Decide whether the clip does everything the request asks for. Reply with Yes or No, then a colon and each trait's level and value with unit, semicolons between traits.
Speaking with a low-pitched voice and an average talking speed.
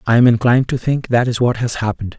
No: low, 115 Hz; fast, 275 wpm